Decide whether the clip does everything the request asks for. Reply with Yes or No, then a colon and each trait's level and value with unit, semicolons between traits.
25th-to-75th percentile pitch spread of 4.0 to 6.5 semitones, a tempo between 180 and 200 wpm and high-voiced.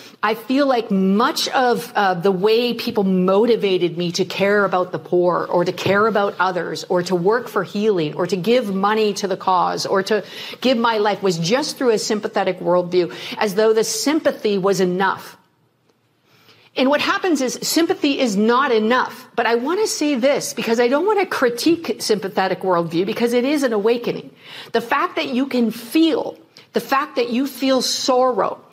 Yes: average, 4.9 semitones; average, 185 wpm; high, 220 Hz